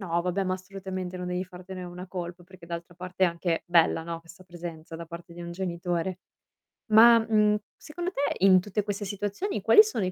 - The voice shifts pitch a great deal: No, narrow, 2.4 semitones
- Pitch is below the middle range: No, medium, 185 Hz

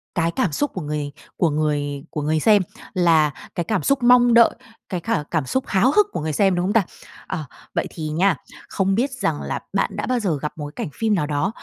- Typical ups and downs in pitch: No, wide, 6.2 semitones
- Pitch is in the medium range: Yes, medium, 175 Hz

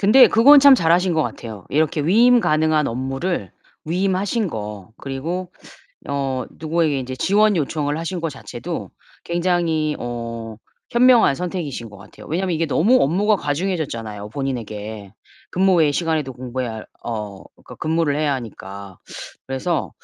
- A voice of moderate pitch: Yes, medium, 155 Hz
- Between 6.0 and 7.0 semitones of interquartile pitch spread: Yes, wide, 6.6 semitones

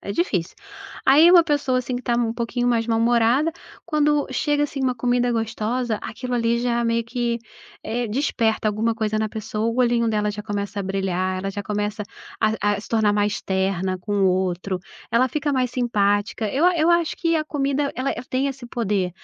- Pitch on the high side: Yes, high, 230 Hz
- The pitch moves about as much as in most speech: Yes, average, 3.6 semitones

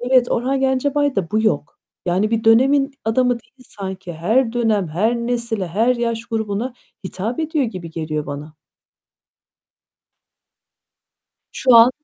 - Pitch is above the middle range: Yes, high, 225 Hz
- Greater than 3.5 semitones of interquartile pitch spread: Yes, average, 4.7 semitones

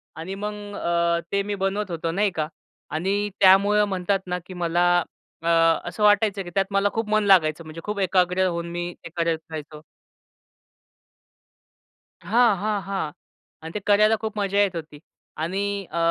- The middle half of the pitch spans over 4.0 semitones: No, average, 3.2 semitones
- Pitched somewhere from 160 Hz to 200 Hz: Yes, high, 190 Hz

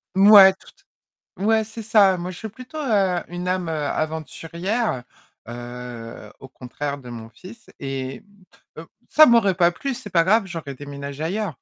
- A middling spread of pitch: No, wide, 7.3 semitones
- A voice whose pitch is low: No, medium, 175 Hz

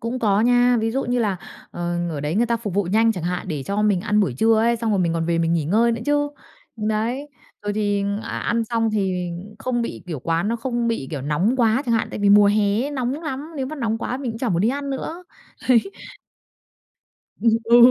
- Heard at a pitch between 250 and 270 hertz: No, high, 225 Hz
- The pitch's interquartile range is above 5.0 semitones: No, average, 4.0 semitones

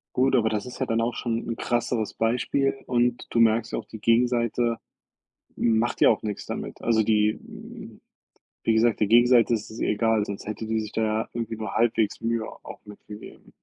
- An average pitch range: No, narrow, 1.5 semitones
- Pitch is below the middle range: Yes, low, 115 Hz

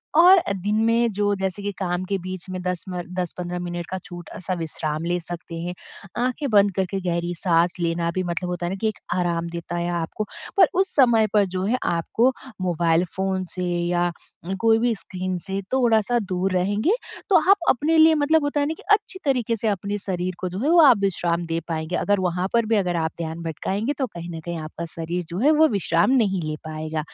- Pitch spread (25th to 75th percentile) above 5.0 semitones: No, average, 4.1 semitones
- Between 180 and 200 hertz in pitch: Yes, medium, 185 Hz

